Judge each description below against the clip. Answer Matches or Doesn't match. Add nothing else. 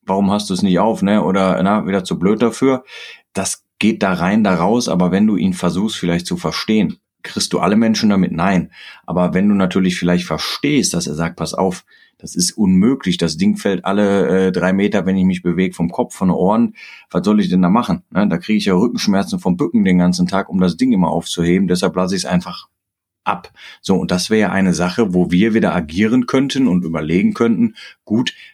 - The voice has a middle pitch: Doesn't match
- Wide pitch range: Doesn't match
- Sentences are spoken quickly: Matches